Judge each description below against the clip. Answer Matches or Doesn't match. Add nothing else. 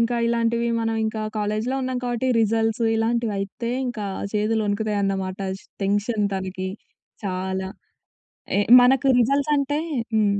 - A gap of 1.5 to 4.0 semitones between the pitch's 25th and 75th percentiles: Matches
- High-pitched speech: Matches